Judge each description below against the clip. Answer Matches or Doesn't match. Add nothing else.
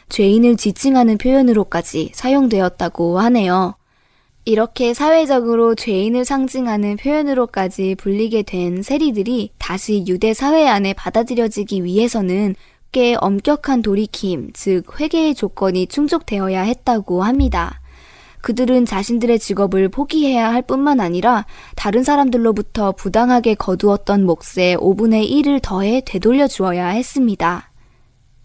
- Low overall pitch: Doesn't match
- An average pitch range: Matches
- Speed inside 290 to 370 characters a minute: Matches